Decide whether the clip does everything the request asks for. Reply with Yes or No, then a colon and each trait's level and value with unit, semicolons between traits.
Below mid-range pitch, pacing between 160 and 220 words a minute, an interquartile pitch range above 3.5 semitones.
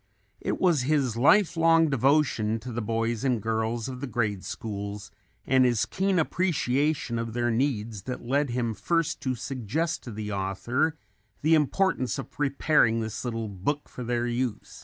Yes: low, 125 Hz; average, 165 wpm; average, 4.5 semitones